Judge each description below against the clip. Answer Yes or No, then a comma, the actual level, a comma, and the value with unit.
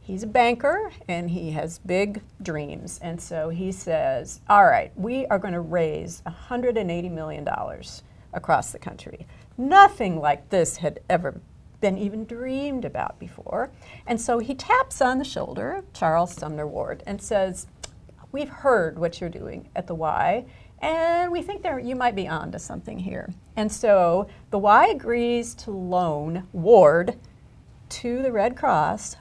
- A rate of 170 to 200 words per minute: No, average, 160 wpm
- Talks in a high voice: Yes, high, 205 Hz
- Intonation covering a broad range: Yes, wide, 6.6 semitones